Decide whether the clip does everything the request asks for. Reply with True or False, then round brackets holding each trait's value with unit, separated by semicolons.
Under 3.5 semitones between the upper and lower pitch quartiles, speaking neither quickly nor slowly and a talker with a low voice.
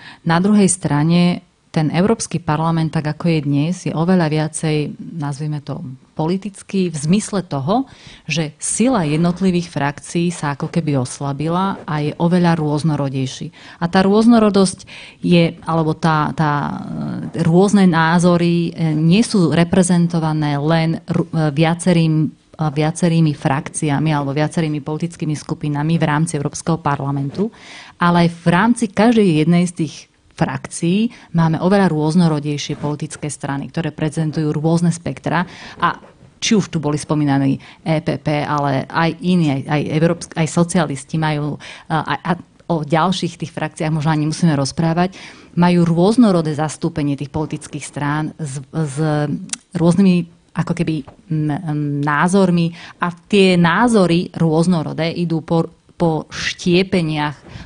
False (2.6 semitones; 125 wpm; 160 Hz)